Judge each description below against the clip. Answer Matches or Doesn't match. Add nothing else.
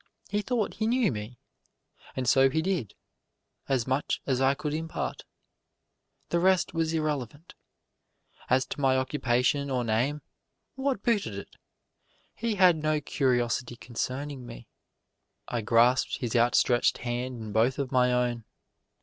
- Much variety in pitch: Doesn't match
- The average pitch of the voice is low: Matches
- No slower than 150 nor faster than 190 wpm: Doesn't match